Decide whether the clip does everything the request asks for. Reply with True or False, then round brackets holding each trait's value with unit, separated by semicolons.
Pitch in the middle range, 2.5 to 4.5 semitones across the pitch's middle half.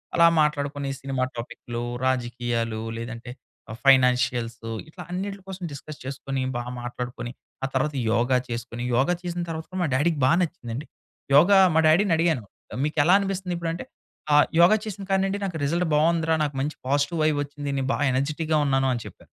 False (145 Hz; 5.0 semitones)